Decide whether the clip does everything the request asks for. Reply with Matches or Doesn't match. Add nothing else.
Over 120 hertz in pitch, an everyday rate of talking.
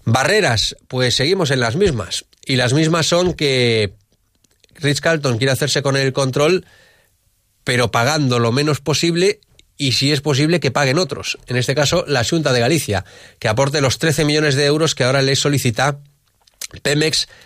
Matches